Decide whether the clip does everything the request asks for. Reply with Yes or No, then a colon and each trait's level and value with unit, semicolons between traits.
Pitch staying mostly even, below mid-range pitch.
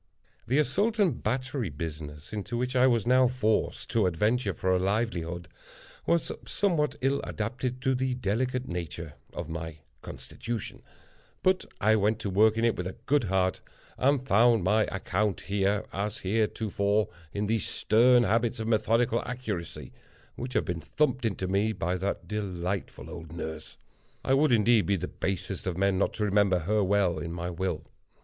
No: average, 4.8 semitones; low, 105 Hz